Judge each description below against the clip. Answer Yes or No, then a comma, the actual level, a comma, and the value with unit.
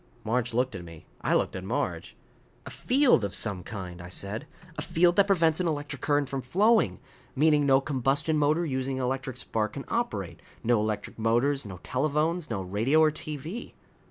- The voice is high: No, low, 135 Hz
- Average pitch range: No, wide, 5.9 semitones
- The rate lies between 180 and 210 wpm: Yes, average, 185 wpm